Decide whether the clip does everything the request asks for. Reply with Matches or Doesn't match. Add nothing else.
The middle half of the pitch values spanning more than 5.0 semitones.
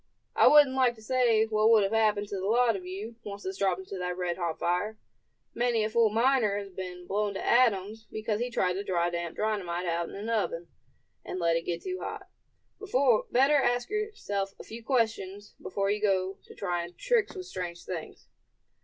Doesn't match